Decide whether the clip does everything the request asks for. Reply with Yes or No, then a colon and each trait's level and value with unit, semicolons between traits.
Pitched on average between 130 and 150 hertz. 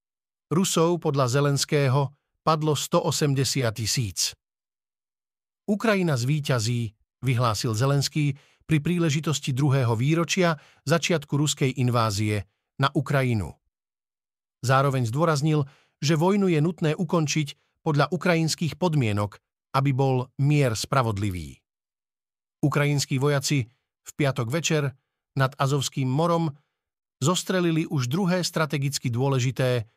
Yes: medium, 140 Hz